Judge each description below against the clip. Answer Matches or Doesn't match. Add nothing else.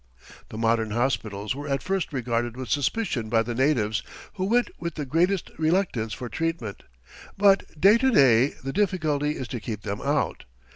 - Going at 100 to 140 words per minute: Doesn't match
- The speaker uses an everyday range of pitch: Doesn't match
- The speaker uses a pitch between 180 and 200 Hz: Doesn't match